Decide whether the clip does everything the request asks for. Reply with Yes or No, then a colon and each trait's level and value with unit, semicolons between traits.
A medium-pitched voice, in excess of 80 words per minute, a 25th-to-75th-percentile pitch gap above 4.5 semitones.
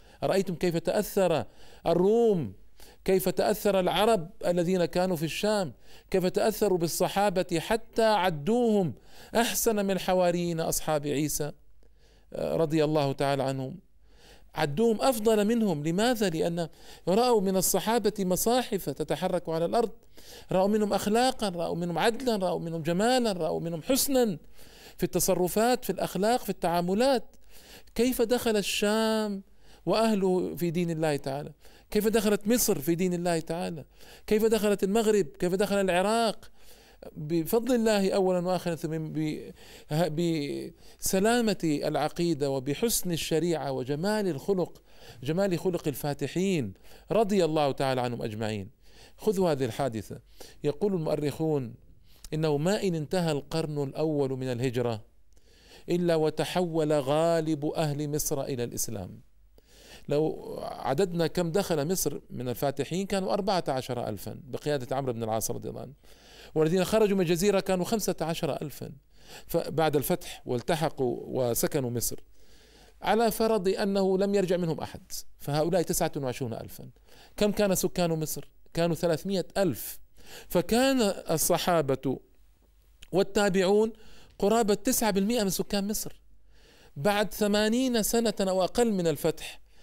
Yes: medium, 175 Hz; average, 120 wpm; average, 5.3 semitones